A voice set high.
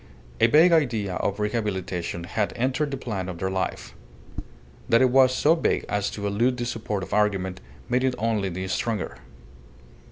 No: low, 105 Hz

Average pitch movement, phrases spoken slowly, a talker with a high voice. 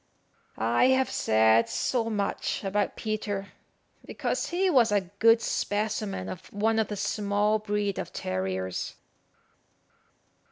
Yes: average, 4.2 semitones; slow, 120 wpm; high, 205 Hz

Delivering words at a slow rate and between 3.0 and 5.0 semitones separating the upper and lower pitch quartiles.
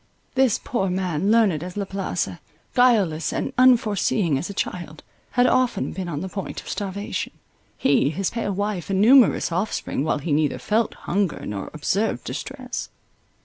No: average, 160 wpm; average, 4.3 semitones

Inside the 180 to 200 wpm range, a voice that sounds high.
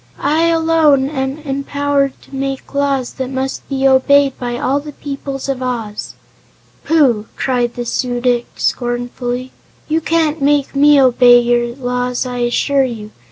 No: average, 150 wpm; very high, 265 Hz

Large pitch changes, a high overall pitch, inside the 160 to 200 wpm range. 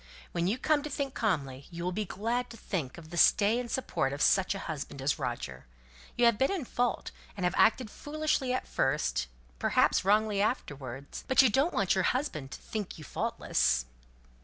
Yes: wide, 8.8 semitones; high, 200 Hz; average, 190 wpm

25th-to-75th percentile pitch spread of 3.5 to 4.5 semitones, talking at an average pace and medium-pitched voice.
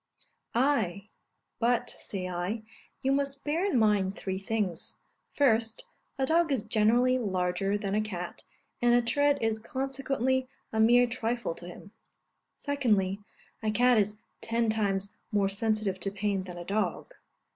No: average, 4.2 semitones; average, 145 wpm; high, 220 Hz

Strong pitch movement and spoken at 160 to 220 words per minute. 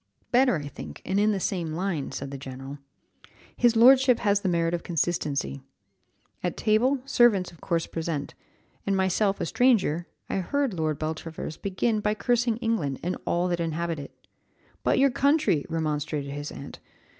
Yes: wide, 6.2 semitones; average, 165 wpm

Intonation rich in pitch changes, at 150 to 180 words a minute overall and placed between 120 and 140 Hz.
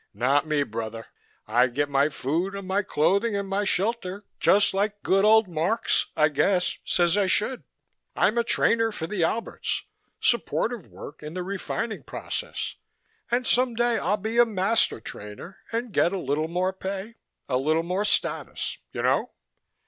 No: wide, 5.8 semitones; average, 165 wpm; high, 190 Hz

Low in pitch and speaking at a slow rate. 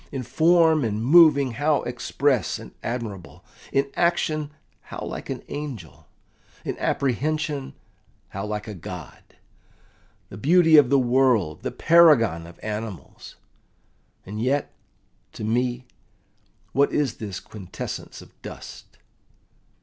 Yes: low, 125 Hz; slow, 120 wpm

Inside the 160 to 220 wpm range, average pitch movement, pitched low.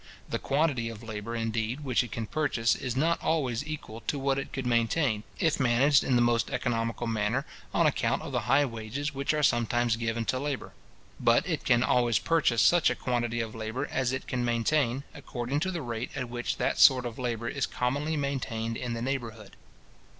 Yes: average, 200 wpm; average, 3.2 semitones; low, 120 Hz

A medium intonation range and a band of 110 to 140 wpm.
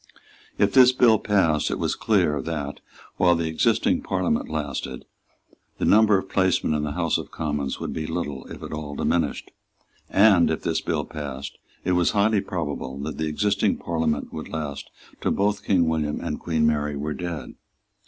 No: average, 4.0 semitones; average, 175 wpm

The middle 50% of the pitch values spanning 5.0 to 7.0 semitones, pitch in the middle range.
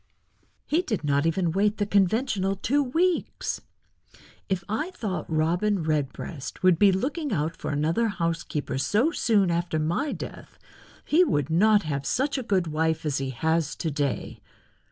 Yes: wide, 5.6 semitones; medium, 180 Hz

